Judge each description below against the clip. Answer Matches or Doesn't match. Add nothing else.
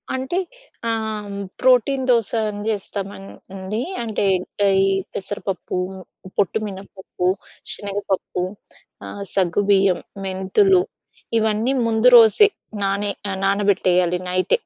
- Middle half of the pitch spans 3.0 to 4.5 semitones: Doesn't match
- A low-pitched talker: Doesn't match